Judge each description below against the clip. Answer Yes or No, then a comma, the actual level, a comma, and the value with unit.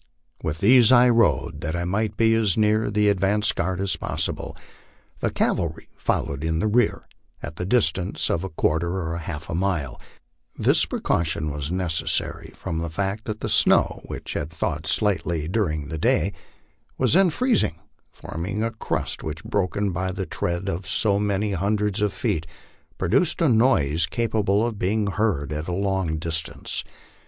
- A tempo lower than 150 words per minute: No, average, 165 wpm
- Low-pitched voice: Yes, very low, 95 Hz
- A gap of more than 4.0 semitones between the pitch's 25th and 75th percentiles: Yes, average, 4.5 semitones